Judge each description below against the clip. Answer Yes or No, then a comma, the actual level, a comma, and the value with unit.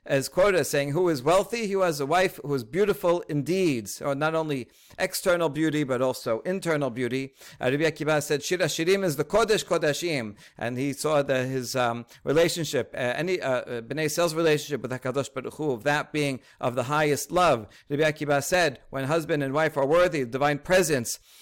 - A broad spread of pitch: No, average, 4.1 semitones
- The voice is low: No, medium, 150 Hz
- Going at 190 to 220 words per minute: Yes, average, 200 wpm